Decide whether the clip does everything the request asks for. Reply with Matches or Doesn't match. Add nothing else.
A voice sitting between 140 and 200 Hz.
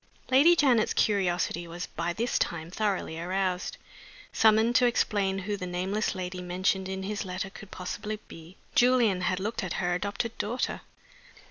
Matches